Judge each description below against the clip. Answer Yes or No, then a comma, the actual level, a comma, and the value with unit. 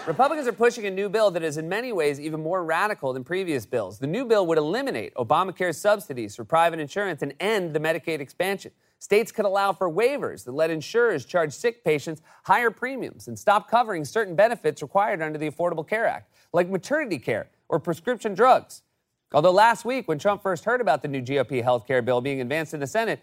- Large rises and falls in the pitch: Yes, wide, 6.1 semitones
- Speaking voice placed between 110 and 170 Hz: No, medium, 180 Hz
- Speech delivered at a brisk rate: Yes, fast, 210 wpm